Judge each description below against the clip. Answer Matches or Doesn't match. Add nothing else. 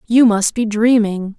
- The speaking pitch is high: Matches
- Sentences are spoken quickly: Doesn't match